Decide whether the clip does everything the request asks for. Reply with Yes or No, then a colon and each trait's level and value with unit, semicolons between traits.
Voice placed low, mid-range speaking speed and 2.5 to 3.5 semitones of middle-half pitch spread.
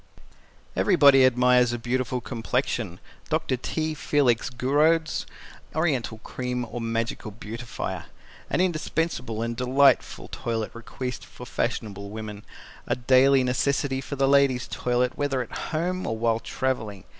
No: low, 125 Hz; slow, 125 wpm; average, 3.1 semitones